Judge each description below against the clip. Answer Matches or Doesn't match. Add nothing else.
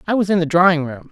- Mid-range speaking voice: Matches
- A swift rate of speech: Matches